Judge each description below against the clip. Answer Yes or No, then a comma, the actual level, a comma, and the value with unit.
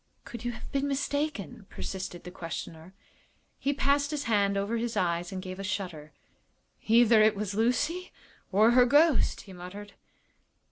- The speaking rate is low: No, average, 155 wpm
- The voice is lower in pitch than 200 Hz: No, high, 215 Hz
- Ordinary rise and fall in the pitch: No, wide, 6.0 semitones